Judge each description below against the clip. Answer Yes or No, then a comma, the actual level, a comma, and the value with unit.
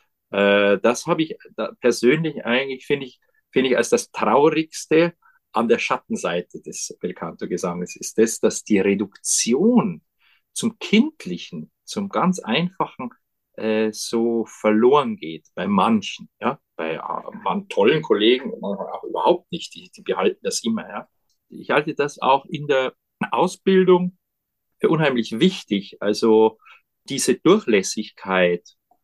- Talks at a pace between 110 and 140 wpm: Yes, average, 130 wpm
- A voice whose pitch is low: No, medium, 155 Hz